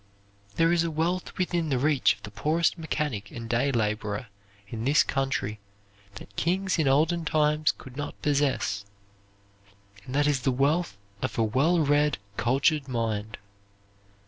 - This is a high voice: No, medium, 140 Hz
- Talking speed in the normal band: Yes, average, 150 wpm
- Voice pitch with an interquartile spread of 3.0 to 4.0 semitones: No, average, 5.1 semitones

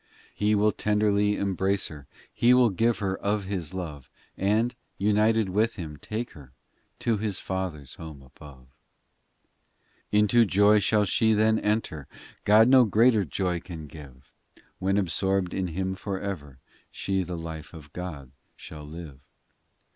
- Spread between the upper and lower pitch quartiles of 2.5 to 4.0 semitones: No, average, 4.7 semitones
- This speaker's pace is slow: No, average, 155 wpm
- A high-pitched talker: No, very low, 95 Hz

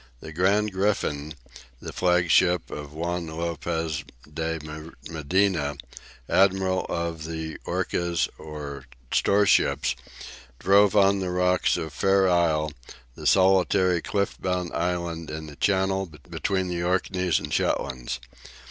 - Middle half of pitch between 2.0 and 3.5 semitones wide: Yes, average, 3.0 semitones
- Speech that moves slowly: Yes, slow, 115 wpm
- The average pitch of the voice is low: Yes, very low, 85 Hz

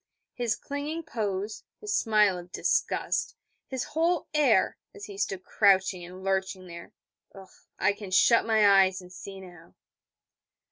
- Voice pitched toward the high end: Yes, high, 200 Hz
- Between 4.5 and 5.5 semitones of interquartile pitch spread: No, average, 3.6 semitones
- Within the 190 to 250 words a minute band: No, average, 140 wpm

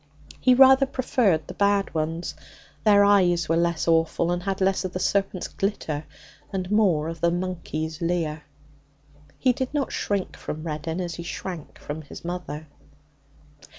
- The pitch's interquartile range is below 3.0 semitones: No, average, 3.6 semitones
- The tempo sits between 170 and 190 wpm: No, average, 155 wpm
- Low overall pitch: No, medium, 175 Hz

